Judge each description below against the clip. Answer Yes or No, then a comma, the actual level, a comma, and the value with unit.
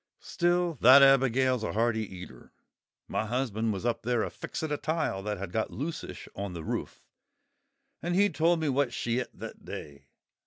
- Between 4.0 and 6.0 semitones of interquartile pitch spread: Yes, wide, 5.4 semitones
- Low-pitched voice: Yes, low, 125 Hz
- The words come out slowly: No, average, 180 wpm